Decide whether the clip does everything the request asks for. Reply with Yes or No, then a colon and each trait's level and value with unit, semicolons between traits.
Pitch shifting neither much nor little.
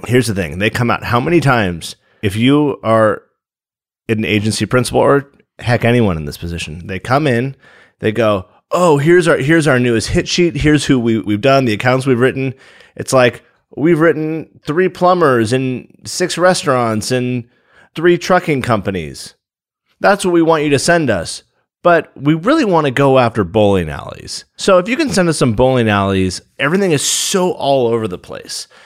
No: wide, 6.4 semitones